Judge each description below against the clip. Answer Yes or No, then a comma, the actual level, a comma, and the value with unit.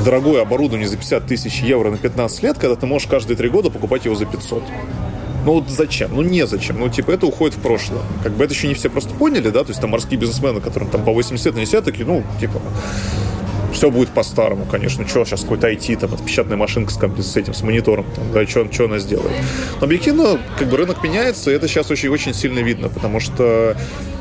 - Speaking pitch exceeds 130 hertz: No, low, 115 Hz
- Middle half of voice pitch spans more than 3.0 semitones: Yes, average, 4.5 semitones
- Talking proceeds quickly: Yes, fast, 220 wpm